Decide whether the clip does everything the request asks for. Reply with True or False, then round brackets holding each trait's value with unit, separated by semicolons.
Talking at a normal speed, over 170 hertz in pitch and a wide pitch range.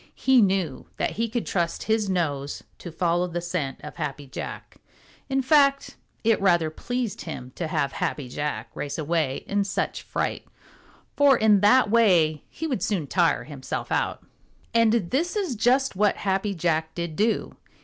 True (165 wpm; 185 Hz; 6.5 semitones)